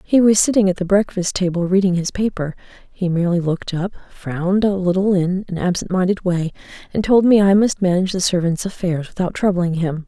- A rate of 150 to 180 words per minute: No, fast, 205 wpm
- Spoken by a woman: Yes, female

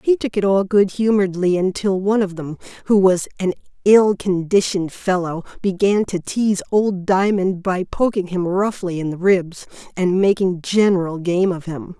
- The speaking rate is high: No, average, 170 wpm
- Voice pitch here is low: No, high, 190 Hz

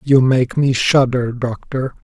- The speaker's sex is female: No, male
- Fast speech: No, average, 140 wpm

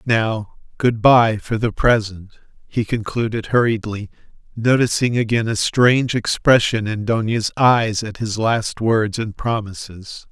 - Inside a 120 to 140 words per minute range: Yes, slow, 135 wpm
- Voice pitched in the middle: No, low, 110 Hz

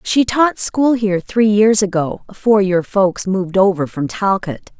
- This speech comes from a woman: Yes, female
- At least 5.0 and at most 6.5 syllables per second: No, 4.6 syllables/s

